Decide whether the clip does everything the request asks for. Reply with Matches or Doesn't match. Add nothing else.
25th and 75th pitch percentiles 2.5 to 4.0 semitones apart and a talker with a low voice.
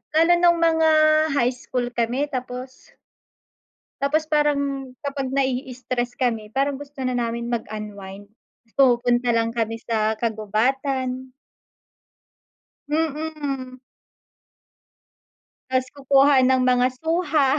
Doesn't match